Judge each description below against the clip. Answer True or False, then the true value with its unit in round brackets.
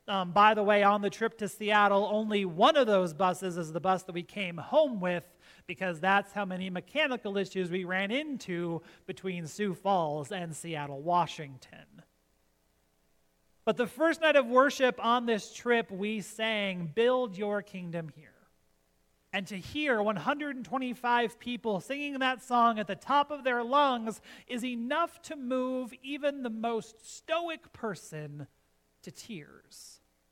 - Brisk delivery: False (150 wpm)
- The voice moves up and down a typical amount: False (5.8 semitones)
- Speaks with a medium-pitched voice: False (205 Hz)